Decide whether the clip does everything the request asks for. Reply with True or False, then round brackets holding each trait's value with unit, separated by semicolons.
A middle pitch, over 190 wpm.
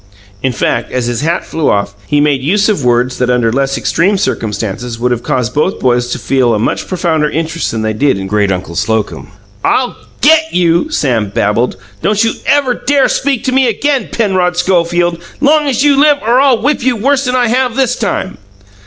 True (170 Hz; 205 wpm)